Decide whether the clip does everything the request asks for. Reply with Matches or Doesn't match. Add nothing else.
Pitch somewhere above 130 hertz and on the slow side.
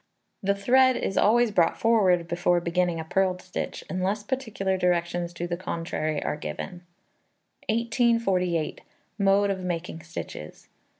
Matches